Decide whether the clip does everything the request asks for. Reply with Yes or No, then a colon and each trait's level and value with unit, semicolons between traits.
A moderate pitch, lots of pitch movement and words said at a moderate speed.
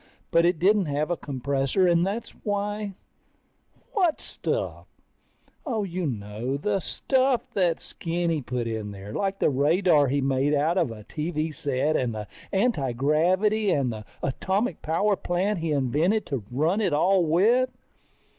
Yes: medium, 165 Hz; wide, 6.3 semitones; average, 150 wpm